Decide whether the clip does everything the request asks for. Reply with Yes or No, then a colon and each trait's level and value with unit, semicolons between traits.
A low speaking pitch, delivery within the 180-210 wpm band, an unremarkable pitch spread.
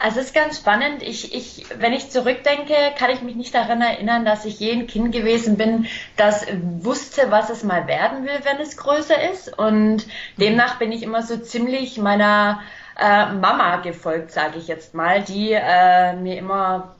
No: high, 225 Hz; average, 185 wpm; average, 3.6 semitones